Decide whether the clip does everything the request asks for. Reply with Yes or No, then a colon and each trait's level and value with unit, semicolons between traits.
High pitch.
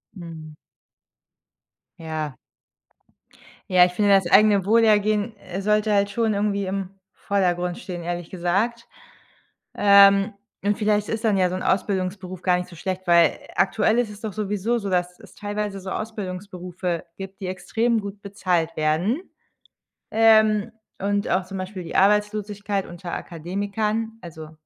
Yes: high, 195 Hz